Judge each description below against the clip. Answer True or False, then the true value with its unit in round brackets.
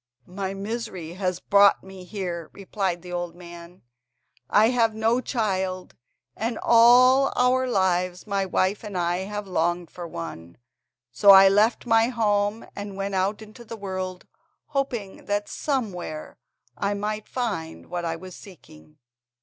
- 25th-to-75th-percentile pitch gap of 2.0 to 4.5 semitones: True (3.5 semitones)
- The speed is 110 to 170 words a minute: True (145 wpm)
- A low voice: False (195 Hz)